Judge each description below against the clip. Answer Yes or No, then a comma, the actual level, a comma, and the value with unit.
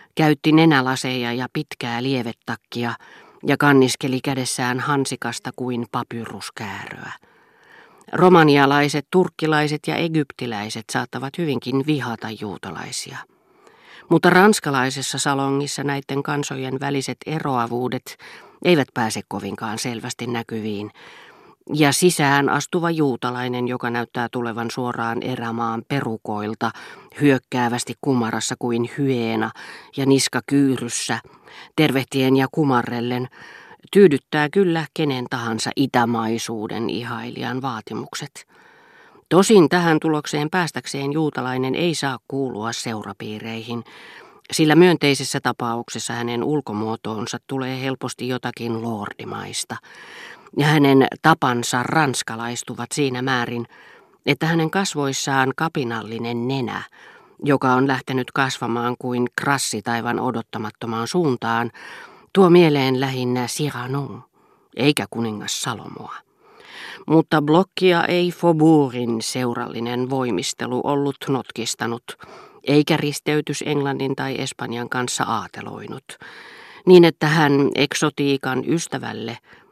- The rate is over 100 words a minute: No, slow, 95 wpm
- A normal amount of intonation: Yes, average, 3.7 semitones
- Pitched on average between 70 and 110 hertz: No, low, 130 Hz